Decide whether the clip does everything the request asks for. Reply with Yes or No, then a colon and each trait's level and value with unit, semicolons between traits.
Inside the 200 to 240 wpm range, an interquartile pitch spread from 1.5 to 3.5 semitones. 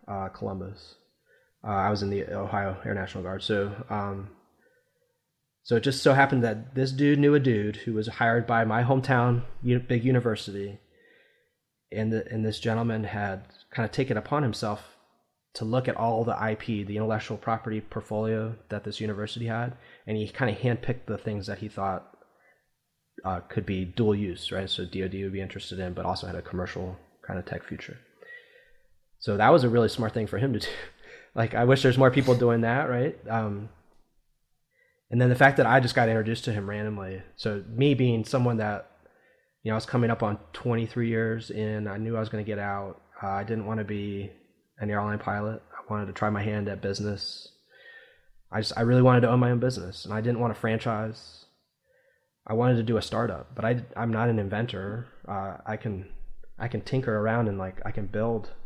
Yes: fast, 205 wpm; average, 2.8 semitones